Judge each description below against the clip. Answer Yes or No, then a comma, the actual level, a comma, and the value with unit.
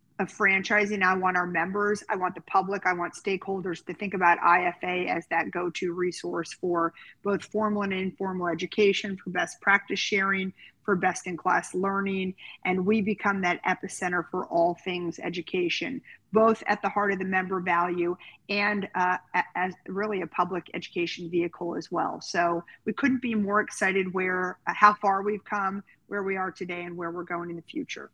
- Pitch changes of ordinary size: No, narrow, 2.3 semitones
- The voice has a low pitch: No, medium, 185 Hz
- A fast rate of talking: No, average, 185 wpm